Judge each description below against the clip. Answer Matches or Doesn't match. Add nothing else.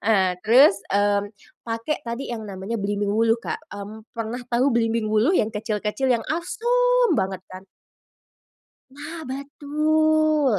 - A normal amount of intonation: Doesn't match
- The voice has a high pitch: Matches